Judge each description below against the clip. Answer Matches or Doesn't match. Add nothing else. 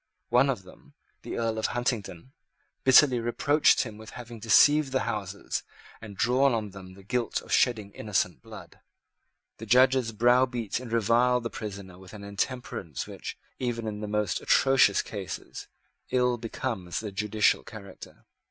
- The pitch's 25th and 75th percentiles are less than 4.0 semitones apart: Matches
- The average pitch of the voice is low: Matches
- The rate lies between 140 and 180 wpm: Matches